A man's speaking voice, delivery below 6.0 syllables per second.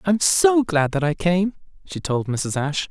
Yes: male; 4.9 syllables/s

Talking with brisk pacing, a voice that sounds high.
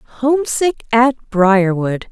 No: slow, 85 wpm; high, 235 Hz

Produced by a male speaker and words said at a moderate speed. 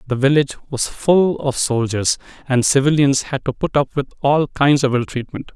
Yes: male; average, 195 wpm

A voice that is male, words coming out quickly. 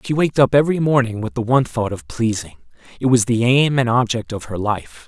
Yes: male; fast, 235 wpm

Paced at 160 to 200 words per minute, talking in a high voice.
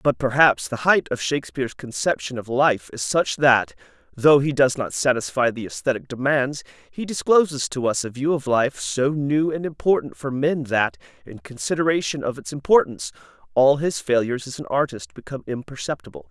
No: average, 175 wpm; low, 130 Hz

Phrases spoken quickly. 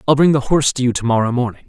Yes: fast, 320 wpm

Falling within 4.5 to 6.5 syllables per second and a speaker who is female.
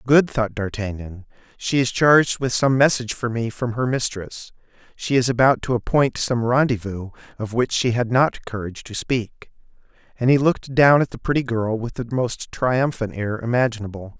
No: 5.0 syllables/s; male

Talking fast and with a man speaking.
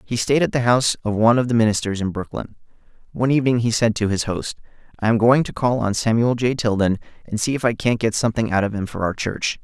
Yes: fast, 255 wpm; male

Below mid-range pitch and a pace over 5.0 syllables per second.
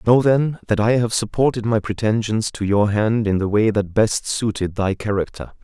No: low, 110 Hz; 4.9 syllables/s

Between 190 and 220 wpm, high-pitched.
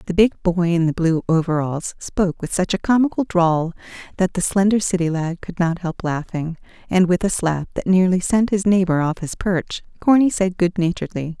No: average, 200 wpm; medium, 180 Hz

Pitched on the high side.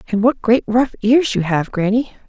Yes: high, 225 Hz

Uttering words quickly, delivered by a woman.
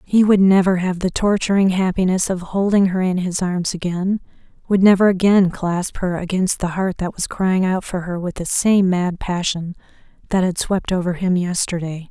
No: average, 195 wpm; female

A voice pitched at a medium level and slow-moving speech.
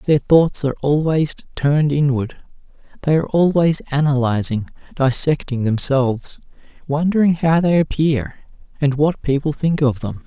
Yes: medium, 145 Hz; slow, 130 wpm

